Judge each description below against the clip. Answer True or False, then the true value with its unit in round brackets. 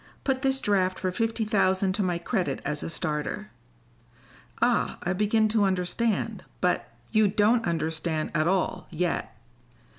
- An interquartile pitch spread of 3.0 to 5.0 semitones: True (4.1 semitones)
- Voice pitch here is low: False (185 Hz)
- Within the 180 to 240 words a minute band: False (150 wpm)